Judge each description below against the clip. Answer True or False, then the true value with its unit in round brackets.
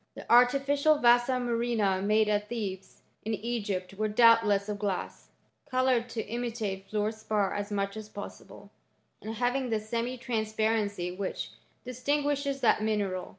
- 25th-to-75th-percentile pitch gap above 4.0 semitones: False (3.0 semitones)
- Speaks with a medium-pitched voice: False (220 Hz)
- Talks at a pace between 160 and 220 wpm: False (150 wpm)